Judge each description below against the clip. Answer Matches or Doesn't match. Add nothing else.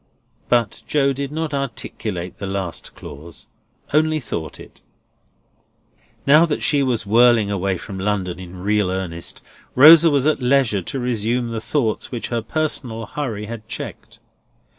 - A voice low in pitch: Matches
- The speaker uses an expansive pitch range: Matches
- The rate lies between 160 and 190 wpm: Doesn't match